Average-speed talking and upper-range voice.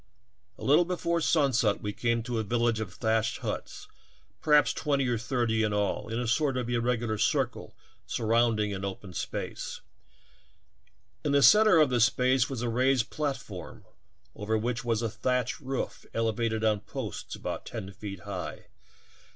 No: average, 160 wpm; low, 120 Hz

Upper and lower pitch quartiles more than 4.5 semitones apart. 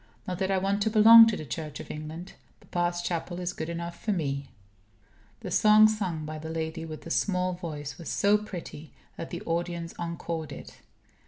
No: average, 3.3 semitones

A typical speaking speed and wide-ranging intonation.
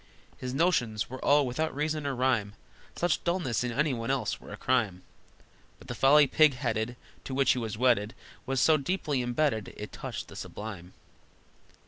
No: average, 175 wpm; average, 4.3 semitones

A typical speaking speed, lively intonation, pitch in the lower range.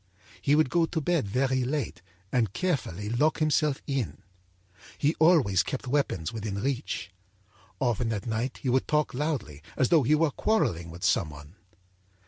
Yes: average, 160 wpm; wide, 6.6 semitones; low, 130 Hz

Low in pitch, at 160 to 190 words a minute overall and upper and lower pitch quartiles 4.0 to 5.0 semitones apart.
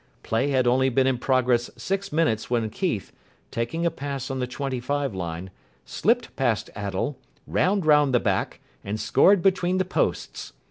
No: low, 130 Hz; average, 170 wpm; wide, 5.4 semitones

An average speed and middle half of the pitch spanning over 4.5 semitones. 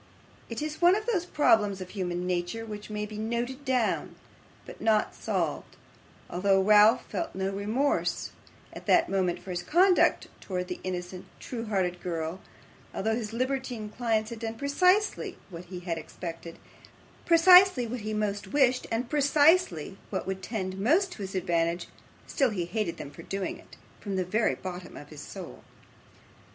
Yes: average, 165 wpm; wide, 5.6 semitones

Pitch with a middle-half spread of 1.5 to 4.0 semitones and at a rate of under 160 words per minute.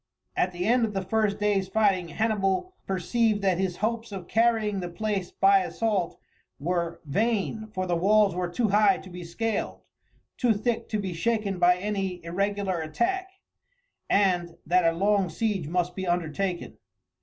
No: average, 3.3 semitones; average, 165 wpm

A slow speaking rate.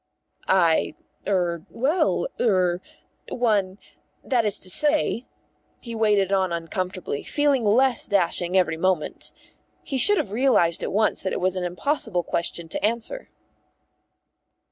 Yes: slow, 130 wpm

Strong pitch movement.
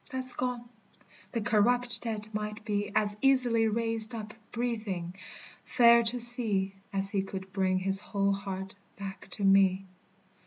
No: average, 3.2 semitones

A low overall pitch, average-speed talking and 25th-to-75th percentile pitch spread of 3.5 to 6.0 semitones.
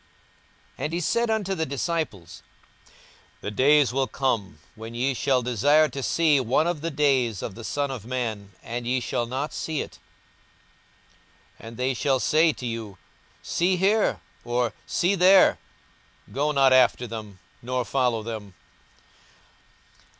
Yes: low, 130 Hz; average, 150 wpm; average, 4.6 semitones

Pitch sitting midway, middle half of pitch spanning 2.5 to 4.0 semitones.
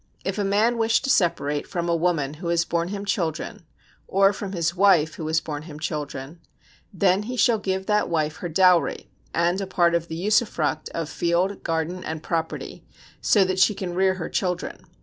Yes: medium, 175 Hz; average, 3.3 semitones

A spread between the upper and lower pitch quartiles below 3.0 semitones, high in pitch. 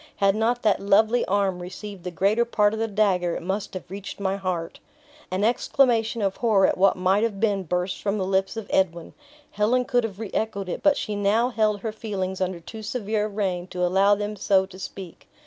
Yes: narrow, 2.5 semitones; high, 200 Hz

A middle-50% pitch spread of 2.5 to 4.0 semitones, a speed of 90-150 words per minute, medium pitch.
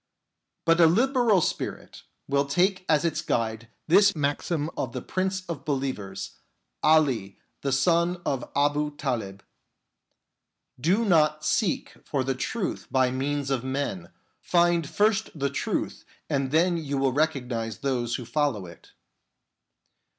No: average, 4.6 semitones; slow, 135 wpm; medium, 145 Hz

